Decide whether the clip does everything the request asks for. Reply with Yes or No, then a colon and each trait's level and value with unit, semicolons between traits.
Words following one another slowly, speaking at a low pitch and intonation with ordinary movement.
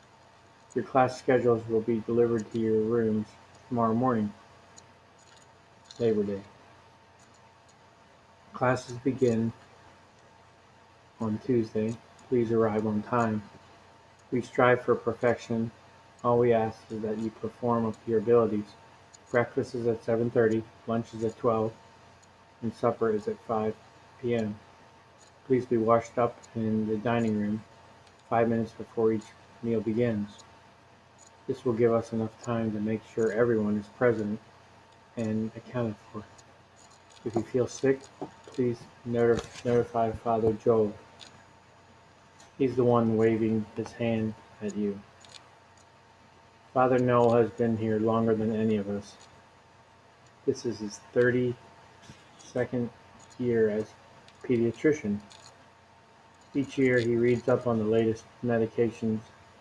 No: slow, 125 wpm; low, 115 Hz; narrow, 1.0 semitones